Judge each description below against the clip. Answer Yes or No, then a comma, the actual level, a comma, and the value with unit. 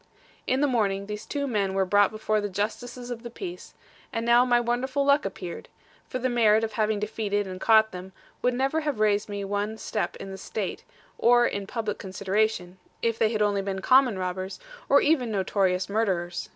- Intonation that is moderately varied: Yes, average, 3.6 semitones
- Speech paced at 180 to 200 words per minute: Yes, average, 195 wpm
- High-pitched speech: Yes, high, 215 Hz